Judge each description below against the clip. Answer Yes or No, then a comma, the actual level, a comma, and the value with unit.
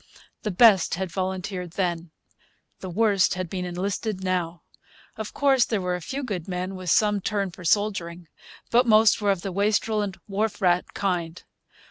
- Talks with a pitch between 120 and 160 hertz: No, high, 190 Hz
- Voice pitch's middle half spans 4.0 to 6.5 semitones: No, average, 2.8 semitones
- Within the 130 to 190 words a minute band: Yes, average, 170 wpm